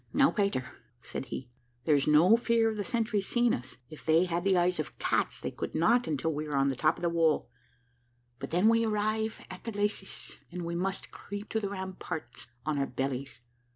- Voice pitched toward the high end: No, medium, 180 Hz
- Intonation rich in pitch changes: Yes, wide, 5.8 semitones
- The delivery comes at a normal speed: No, fast, 215 wpm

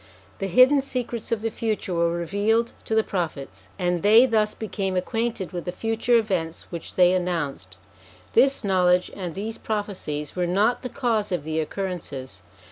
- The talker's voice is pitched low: No, high, 195 Hz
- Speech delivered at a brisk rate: No, average, 170 wpm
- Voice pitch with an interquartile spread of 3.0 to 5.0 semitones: Yes, average, 4.4 semitones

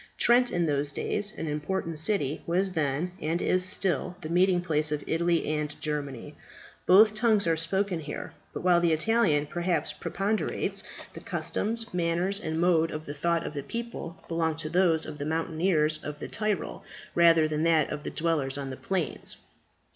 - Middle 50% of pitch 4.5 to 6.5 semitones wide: No, average, 3.3 semitones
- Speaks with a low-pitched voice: No, medium, 165 Hz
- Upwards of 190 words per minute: No, average, 170 wpm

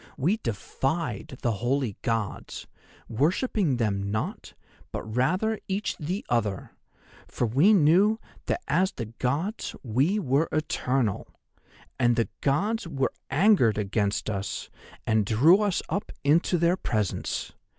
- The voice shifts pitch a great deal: Yes, wide, 8.2 semitones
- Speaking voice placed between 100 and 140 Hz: Yes, low, 135 Hz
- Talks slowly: Yes, slow, 125 wpm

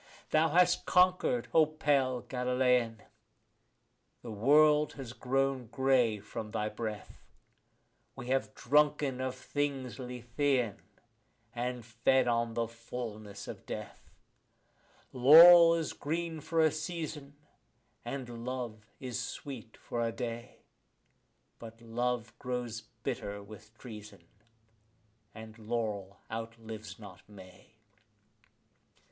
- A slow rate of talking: Yes, slow, 105 wpm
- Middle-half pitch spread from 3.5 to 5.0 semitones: Yes, average, 3.8 semitones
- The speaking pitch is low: Yes, low, 125 Hz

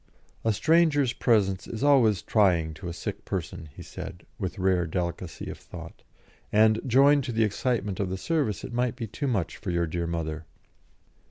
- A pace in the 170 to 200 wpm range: Yes, average, 180 wpm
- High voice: No, low, 105 Hz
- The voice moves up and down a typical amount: No, wide, 5.9 semitones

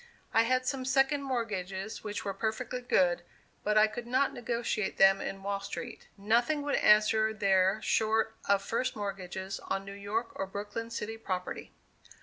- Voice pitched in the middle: No, high, 215 Hz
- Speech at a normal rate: Yes, average, 160 wpm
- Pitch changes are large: No, average, 3.3 semitones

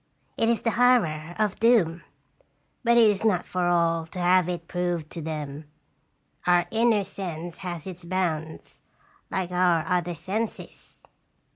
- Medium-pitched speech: Yes, medium, 180 Hz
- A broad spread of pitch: No, average, 3.4 semitones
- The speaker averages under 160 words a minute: Yes, average, 145 wpm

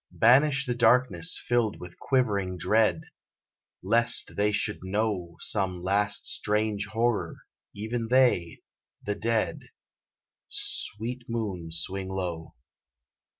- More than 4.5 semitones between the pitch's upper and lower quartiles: No, average, 3.8 semitones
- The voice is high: No, low, 105 Hz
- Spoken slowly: Yes, slow, 105 wpm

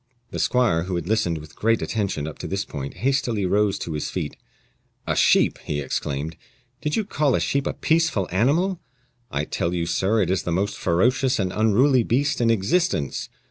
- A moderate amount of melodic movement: No, wide, 7.2 semitones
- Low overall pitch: Yes, low, 105 Hz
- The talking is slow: No, average, 190 wpm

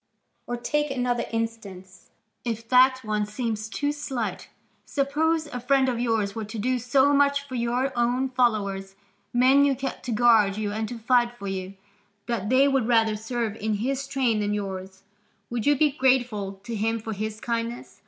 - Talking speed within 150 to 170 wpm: No, average, 180 wpm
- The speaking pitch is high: Yes, high, 235 Hz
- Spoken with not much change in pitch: No, average, 3.5 semitones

